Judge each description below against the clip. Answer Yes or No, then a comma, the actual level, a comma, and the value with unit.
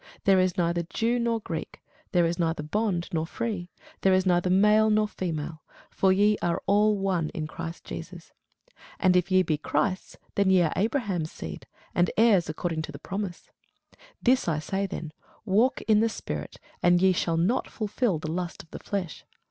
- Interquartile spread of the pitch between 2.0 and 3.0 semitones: No, average, 3.7 semitones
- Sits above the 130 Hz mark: Yes, medium, 185 Hz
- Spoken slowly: No, average, 185 wpm